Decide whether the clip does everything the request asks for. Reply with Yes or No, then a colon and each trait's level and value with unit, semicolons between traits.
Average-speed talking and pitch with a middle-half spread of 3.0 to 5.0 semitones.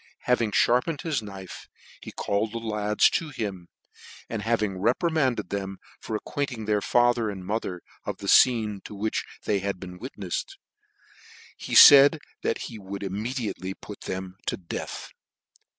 Yes: average, 150 wpm; average, 3.8 semitones